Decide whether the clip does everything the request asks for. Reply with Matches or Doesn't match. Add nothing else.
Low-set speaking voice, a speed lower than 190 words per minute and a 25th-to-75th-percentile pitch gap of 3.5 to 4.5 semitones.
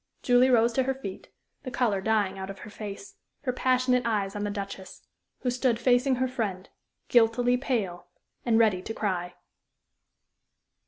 Doesn't match